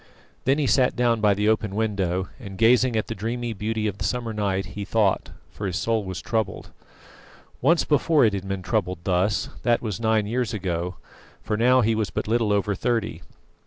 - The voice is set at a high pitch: No, low, 110 Hz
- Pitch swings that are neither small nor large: Yes, average, 3.1 semitones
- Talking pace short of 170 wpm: No, average, 200 wpm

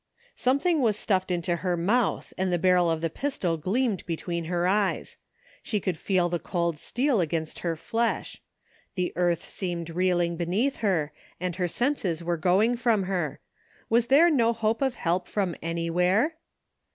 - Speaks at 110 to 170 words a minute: Yes, average, 165 wpm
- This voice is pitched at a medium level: Yes, medium, 180 Hz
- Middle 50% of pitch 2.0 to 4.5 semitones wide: No, average, 4.9 semitones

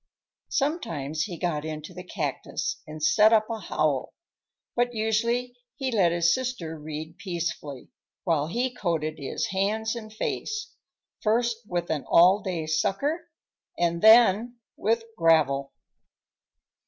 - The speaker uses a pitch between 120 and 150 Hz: No, medium, 185 Hz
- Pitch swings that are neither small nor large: No, wide, 6.5 semitones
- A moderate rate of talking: No, slow, 130 wpm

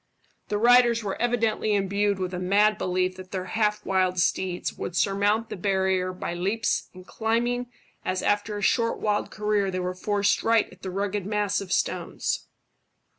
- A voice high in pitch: Yes, high, 200 Hz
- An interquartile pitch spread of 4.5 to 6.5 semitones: No, narrow, 2.4 semitones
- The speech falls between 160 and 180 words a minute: Yes, average, 175 wpm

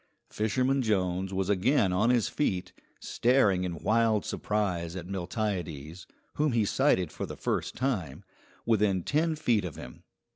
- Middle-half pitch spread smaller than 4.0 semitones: No, average, 4.5 semitones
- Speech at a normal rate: Yes, average, 145 wpm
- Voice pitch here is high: No, low, 100 Hz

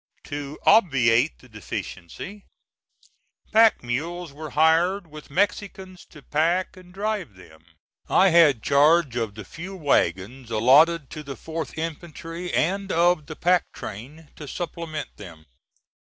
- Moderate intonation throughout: Yes, average, 4.9 semitones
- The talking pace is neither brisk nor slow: No, slow, 130 wpm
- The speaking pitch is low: No, medium, 155 Hz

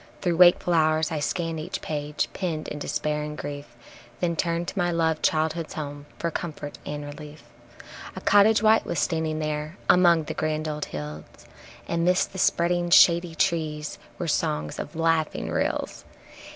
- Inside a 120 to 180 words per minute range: Yes, average, 165 wpm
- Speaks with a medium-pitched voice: Yes, medium, 160 Hz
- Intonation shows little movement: Yes, narrow, 2.3 semitones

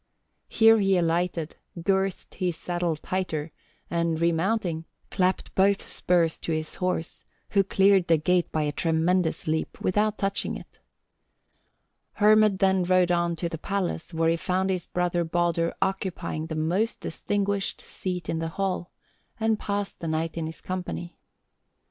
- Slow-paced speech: No, average, 150 wpm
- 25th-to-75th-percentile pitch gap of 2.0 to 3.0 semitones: Yes, average, 2.7 semitones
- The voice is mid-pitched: Yes, medium, 180 Hz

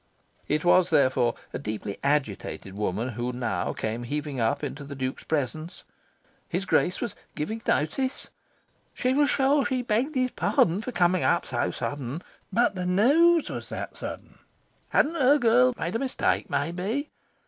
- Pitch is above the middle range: No, medium, 175 Hz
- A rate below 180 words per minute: Yes, average, 160 wpm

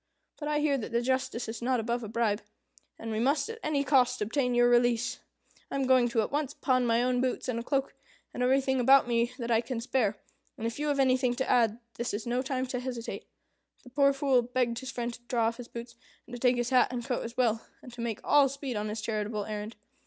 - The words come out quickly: Yes, fast, 245 wpm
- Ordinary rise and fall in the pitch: No, narrow, 2.1 semitones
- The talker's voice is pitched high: Yes, high, 245 Hz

